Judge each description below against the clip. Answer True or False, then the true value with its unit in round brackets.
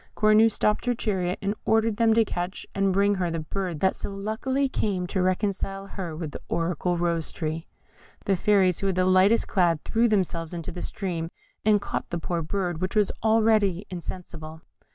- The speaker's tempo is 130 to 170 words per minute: False (195 wpm)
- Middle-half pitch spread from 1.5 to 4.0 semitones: True (3.4 semitones)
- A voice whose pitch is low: False (190 Hz)